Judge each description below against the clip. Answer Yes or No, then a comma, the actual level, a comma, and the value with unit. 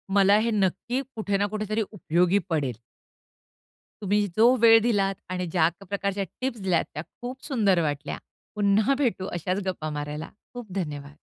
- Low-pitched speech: No, high, 200 Hz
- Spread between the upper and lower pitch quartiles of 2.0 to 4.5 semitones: Yes, average, 4.0 semitones